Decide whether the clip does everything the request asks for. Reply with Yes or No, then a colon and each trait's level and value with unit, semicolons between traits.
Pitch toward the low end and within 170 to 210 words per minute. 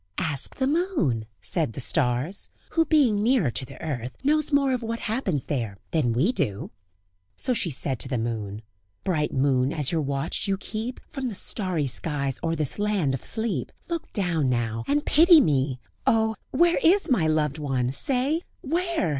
No: medium, 165 Hz; average, 180 wpm